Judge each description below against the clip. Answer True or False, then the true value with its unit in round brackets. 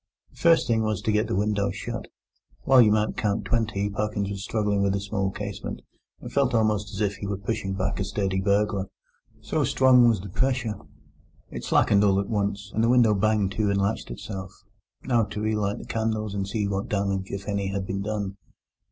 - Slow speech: False (205 wpm)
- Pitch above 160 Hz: False (100 Hz)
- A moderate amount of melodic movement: False (1.7 semitones)